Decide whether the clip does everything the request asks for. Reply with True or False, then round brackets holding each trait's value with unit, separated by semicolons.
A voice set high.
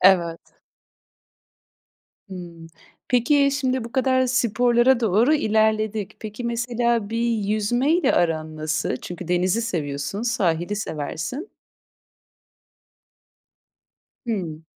True (220 Hz)